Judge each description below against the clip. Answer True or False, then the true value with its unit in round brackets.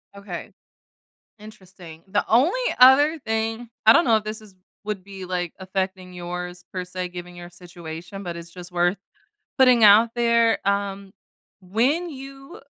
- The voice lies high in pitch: True (195 Hz)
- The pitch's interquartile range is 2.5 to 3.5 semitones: False (4.2 semitones)